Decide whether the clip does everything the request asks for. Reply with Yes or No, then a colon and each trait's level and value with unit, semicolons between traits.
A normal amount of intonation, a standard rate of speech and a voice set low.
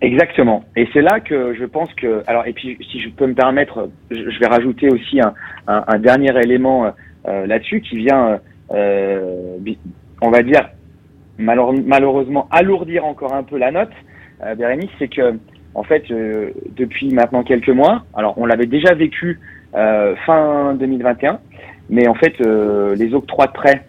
Yes: average, 3.8 semitones; average, 170 wpm; low, 125 Hz